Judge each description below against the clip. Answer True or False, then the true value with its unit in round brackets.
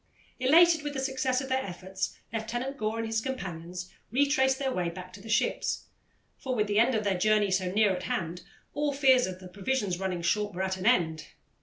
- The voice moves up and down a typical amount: False (6.1 semitones)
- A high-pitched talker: True (215 Hz)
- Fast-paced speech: True (210 wpm)